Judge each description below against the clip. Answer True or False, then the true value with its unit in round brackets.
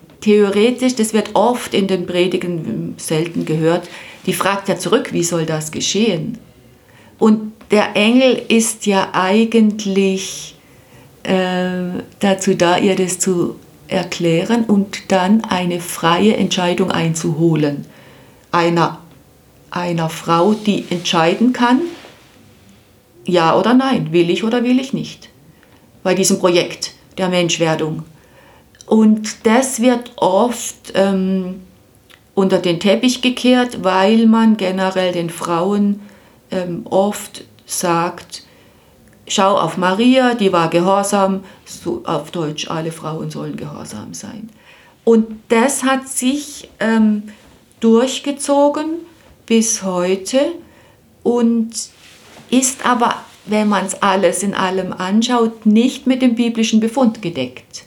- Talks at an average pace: False (115 wpm)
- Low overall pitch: False (190 Hz)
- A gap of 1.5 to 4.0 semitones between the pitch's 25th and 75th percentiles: False (4.7 semitones)